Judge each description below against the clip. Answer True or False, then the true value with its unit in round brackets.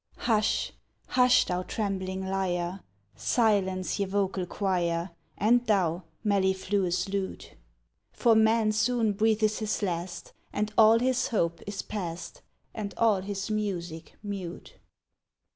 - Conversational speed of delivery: False (115 wpm)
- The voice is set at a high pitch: True (200 Hz)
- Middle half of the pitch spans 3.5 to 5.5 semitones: False (2.7 semitones)